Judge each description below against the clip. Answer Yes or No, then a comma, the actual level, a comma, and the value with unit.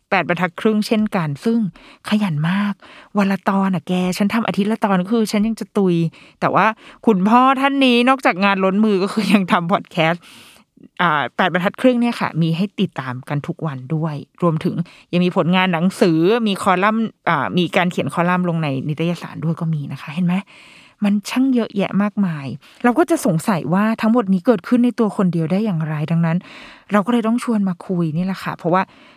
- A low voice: No, high, 195 Hz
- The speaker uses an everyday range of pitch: Yes, average, 4.2 semitones